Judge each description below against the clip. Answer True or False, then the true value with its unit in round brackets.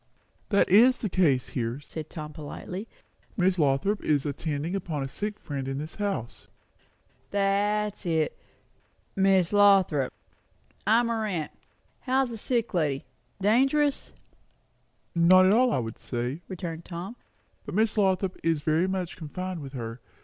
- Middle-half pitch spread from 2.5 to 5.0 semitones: False (5.5 semitones)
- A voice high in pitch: False (180 Hz)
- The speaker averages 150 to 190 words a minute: False (140 wpm)